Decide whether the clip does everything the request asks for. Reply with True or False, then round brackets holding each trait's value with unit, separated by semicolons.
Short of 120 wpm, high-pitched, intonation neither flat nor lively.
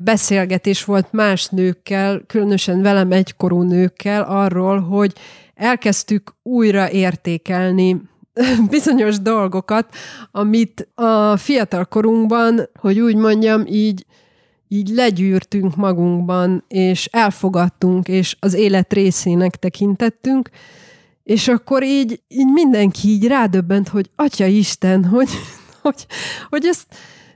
True (105 wpm; 200 Hz; 3.1 semitones)